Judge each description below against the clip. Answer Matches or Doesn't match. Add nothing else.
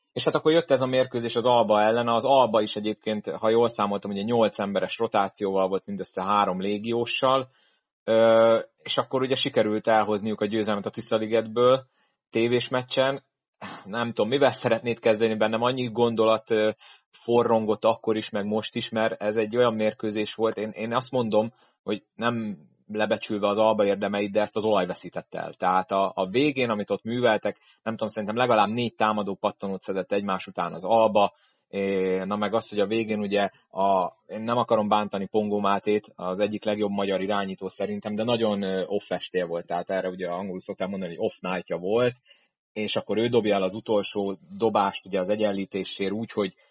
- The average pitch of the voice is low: Matches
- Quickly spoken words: Matches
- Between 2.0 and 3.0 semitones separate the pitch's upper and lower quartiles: Matches